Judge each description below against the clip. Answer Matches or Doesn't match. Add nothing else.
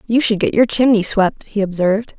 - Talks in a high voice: Matches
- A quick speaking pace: Matches